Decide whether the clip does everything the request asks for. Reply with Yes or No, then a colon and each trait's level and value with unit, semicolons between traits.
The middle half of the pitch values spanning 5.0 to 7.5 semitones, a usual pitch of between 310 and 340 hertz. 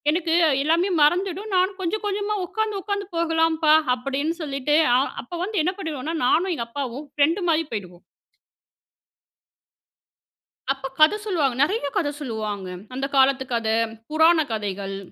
Yes: wide, 5.4 semitones; very high, 315 Hz